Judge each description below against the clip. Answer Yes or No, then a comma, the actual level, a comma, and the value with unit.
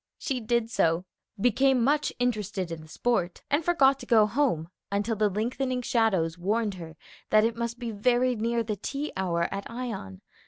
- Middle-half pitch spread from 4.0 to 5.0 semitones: Yes, average, 4.4 semitones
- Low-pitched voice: No, high, 225 Hz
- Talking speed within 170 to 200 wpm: Yes, average, 180 wpm